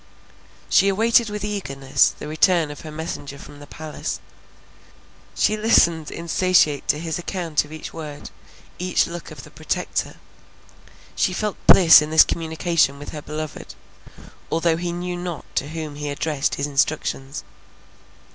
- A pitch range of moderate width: Yes, average, 3.1 semitones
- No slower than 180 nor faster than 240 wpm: No, average, 145 wpm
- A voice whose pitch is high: No, medium, 160 Hz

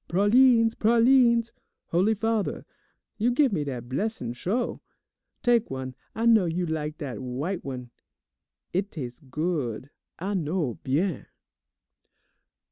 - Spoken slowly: Yes, slow, 120 wpm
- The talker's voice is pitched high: No, medium, 180 Hz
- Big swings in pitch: Yes, wide, 8.5 semitones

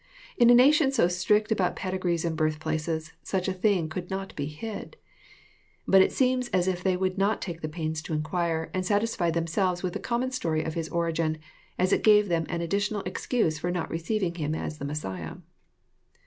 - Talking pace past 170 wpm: Yes, average, 195 wpm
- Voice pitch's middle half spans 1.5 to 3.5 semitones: No, average, 3.9 semitones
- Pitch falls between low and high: Yes, medium, 175 Hz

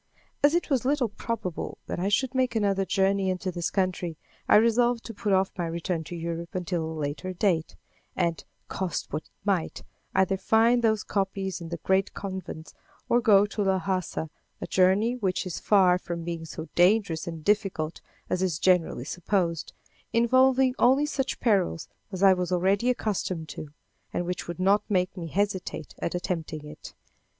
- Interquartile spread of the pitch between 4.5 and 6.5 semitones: No, average, 3.5 semitones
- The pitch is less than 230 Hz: Yes, high, 190 Hz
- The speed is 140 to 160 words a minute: No, average, 175 wpm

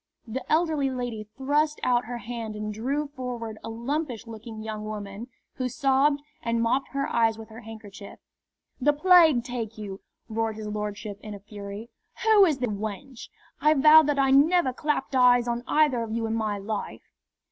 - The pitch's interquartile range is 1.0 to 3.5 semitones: No, average, 4.3 semitones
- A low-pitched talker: No, high, 235 Hz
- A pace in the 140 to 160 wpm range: No, average, 180 wpm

